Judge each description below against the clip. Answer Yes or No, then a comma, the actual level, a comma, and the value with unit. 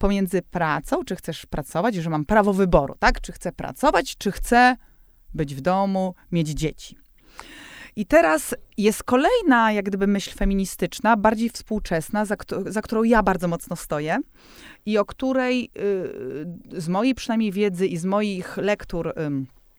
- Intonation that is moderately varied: Yes, average, 3.9 semitones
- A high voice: Yes, high, 200 Hz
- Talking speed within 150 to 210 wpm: Yes, average, 155 wpm